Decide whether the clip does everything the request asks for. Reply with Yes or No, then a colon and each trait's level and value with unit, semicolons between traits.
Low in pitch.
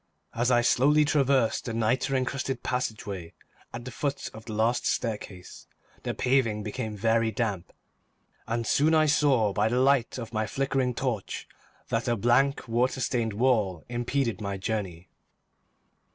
Yes: low, 120 Hz